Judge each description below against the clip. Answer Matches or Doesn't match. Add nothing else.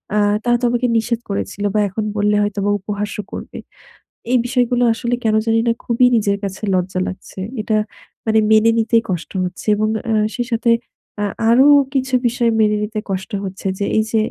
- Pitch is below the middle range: Doesn't match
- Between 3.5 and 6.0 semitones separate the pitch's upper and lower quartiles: Doesn't match